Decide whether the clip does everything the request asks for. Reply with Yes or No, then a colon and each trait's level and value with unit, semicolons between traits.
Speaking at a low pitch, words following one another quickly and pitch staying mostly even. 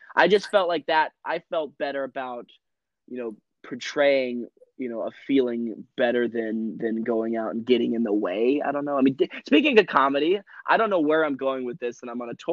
No: low, 125 Hz; fast, 230 wpm; average, 3.4 semitones